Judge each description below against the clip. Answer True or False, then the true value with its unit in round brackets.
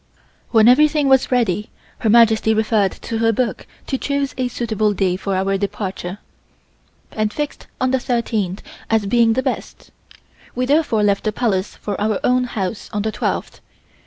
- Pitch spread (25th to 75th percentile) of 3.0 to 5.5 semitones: True (3.5 semitones)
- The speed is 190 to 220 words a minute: False (165 wpm)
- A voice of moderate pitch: False (220 Hz)